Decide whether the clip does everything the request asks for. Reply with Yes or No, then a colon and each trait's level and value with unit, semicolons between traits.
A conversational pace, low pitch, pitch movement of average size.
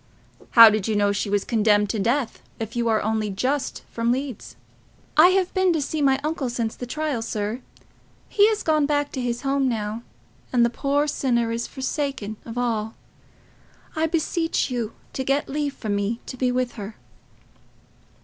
No: average, 180 wpm; high, 245 Hz; average, 4.3 semitones